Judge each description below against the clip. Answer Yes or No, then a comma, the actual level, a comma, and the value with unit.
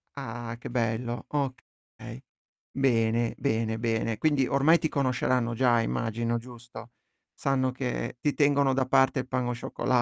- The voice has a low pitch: Yes, low, 125 Hz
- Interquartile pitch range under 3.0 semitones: Yes, narrow, 2.5 semitones